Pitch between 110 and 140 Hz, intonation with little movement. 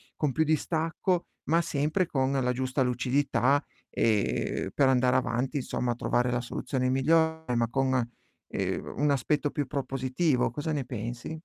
No: low, 135 Hz; average, 3.1 semitones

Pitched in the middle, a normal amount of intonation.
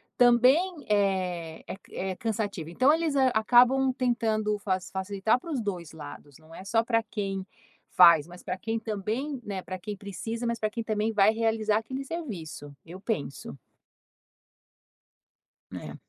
No: high, 215 Hz; average, 4.2 semitones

